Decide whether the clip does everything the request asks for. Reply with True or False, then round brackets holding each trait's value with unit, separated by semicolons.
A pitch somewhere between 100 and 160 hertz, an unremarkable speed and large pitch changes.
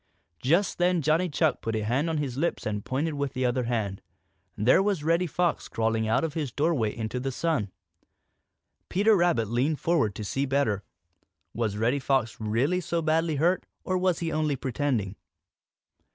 True (140 Hz; 175 wpm; 6.4 semitones)